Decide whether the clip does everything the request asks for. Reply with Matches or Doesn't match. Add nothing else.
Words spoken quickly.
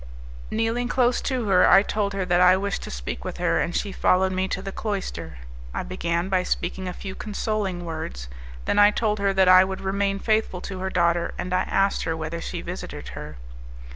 Matches